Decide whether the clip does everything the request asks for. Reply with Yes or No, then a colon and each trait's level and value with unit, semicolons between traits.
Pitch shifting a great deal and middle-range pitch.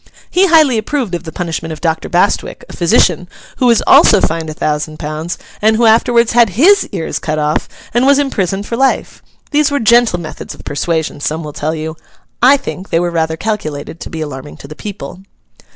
Yes: wide, 6.9 semitones; medium, 175 Hz